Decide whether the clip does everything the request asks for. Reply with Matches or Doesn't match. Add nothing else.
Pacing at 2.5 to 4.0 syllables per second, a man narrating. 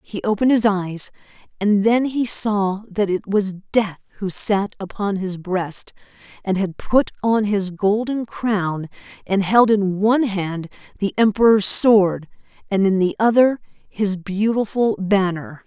Doesn't match